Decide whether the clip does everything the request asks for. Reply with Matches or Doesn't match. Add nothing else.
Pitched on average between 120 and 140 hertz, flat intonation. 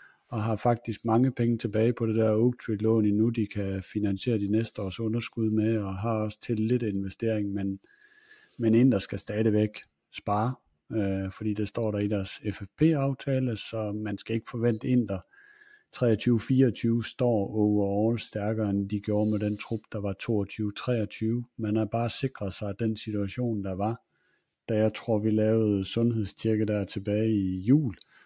Doesn't match